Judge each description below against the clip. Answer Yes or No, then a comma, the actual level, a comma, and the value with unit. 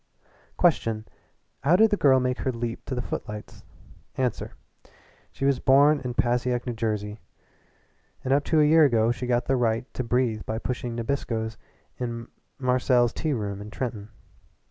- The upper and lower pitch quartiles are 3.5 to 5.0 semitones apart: No, average, 2.8 semitones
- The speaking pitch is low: Yes, low, 125 Hz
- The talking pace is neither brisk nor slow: Yes, average, 165 wpm